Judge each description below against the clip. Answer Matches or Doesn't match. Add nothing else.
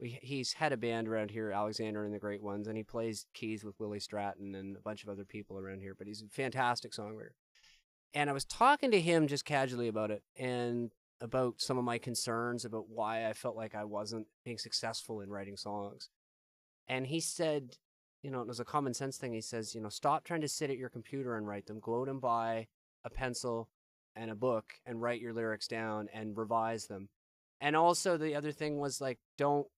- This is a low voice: Matches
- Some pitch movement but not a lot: Matches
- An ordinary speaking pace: Doesn't match